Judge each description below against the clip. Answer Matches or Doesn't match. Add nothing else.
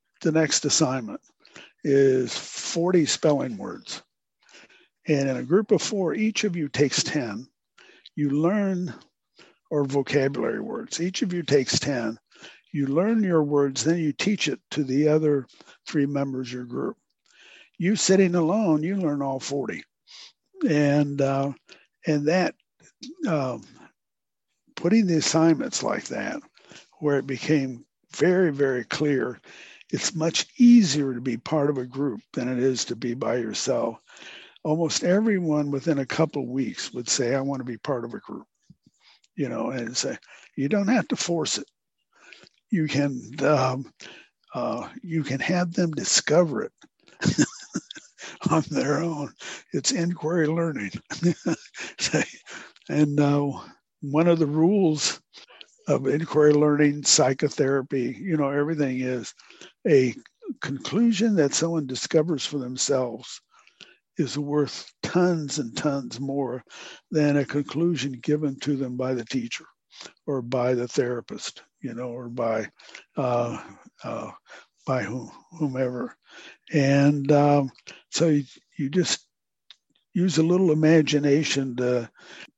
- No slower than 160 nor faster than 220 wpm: Doesn't match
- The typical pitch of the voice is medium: Matches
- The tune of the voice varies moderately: Matches